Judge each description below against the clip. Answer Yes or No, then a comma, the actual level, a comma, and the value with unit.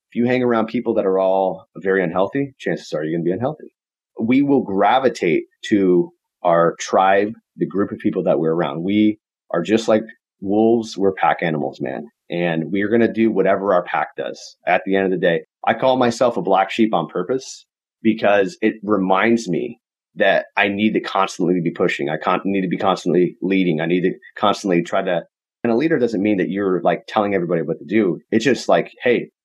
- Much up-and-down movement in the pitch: No, average, 3.7 semitones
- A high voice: No, low, 100 Hz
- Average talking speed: No, fast, 210 wpm